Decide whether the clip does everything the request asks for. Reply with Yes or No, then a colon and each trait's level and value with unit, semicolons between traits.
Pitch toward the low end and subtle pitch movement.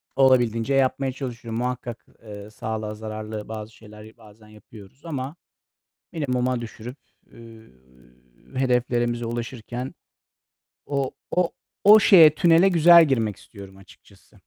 No: low, 120 Hz; average, 3.7 semitones